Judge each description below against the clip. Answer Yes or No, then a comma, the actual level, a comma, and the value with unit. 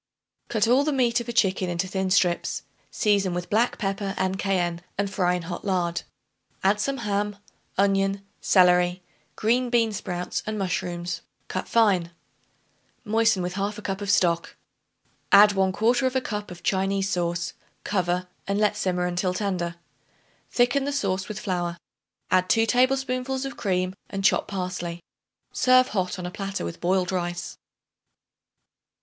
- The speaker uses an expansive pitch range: No, average, 3.0 semitones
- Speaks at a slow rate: No, average, 150 wpm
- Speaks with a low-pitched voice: No, high, 195 Hz